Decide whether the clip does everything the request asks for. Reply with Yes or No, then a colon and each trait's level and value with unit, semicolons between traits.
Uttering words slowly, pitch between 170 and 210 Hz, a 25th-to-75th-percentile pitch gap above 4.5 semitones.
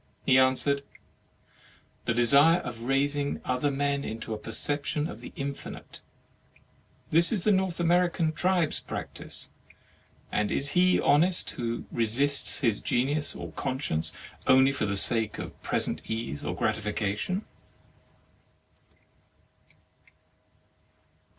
No: slow, 110 wpm; medium, 140 Hz; average, 5.2 semitones